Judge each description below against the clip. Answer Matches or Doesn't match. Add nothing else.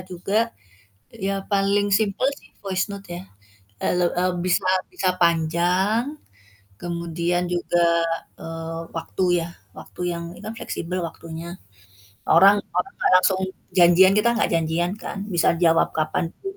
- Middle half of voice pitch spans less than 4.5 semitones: Matches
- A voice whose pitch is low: Doesn't match